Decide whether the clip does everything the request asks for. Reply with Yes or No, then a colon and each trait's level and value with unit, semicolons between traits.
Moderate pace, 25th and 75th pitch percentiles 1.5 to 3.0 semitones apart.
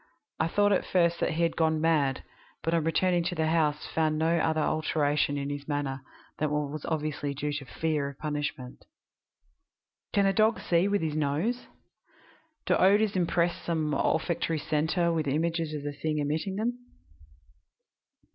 Yes: average, 165 wpm; narrow, 2.4 semitones